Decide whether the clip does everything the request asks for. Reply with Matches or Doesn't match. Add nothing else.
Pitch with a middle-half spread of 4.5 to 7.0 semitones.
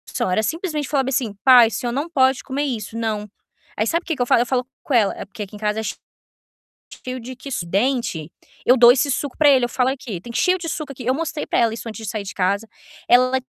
Doesn't match